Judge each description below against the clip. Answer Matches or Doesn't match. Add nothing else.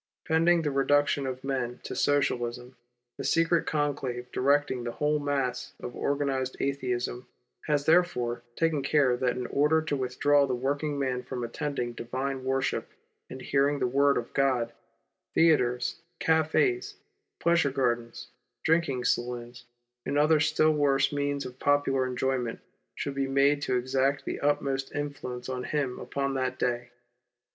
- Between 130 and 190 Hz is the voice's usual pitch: Matches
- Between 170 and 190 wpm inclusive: Doesn't match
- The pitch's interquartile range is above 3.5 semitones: Doesn't match